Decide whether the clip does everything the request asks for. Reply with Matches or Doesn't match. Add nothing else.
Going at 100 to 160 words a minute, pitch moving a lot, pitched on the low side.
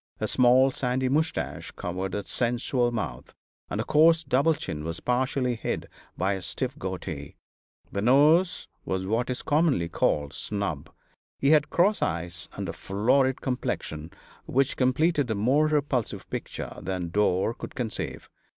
Matches